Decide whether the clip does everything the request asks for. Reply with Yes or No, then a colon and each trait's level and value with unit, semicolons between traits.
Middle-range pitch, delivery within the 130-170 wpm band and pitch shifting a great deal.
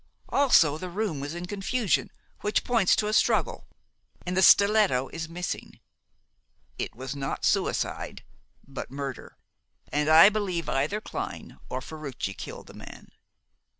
Yes: medium, 170 Hz; average, 140 wpm; wide, 6.4 semitones